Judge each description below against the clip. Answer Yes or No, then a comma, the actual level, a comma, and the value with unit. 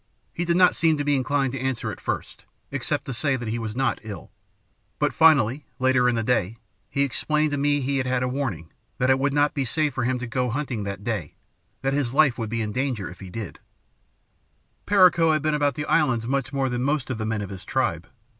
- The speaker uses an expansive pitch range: No, average, 3.8 semitones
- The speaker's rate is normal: No, fast, 245 wpm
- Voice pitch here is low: Yes, low, 130 Hz